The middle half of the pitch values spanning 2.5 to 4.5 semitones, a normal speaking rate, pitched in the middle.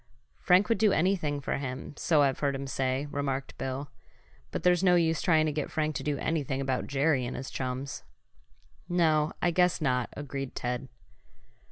Yes: average, 3.4 semitones; average, 180 wpm; medium, 145 Hz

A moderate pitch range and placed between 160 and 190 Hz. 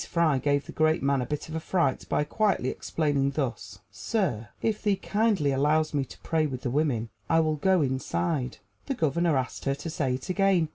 No: average, 3.8 semitones; medium, 150 Hz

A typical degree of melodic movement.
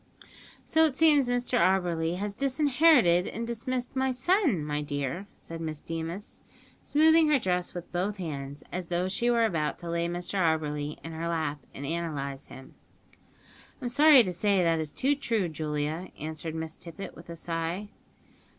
No: wide, 6.9 semitones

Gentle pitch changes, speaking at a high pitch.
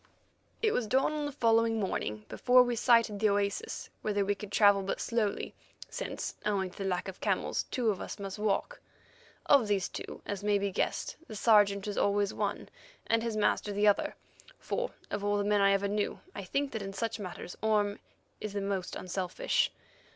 Yes: narrow, 2.2 semitones; high, 205 Hz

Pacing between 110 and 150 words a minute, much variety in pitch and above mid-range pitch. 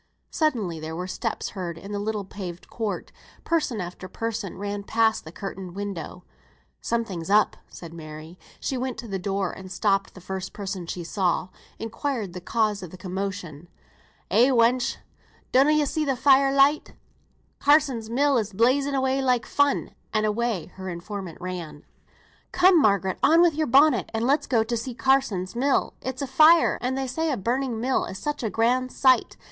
No: average, 175 wpm; wide, 5.9 semitones; high, 220 Hz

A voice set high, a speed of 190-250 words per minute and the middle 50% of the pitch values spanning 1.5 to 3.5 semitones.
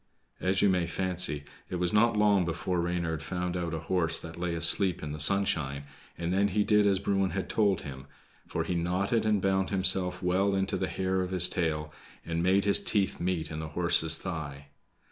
No: very low, 90 Hz; average, 200 wpm; average, 2.7 semitones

